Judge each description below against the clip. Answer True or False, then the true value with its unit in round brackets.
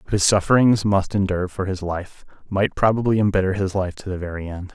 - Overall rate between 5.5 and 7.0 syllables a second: True (5.9 syllables/s)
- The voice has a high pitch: False (95 Hz)